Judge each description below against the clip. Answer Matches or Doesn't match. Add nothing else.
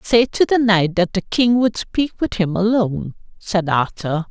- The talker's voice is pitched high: Matches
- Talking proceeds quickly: Doesn't match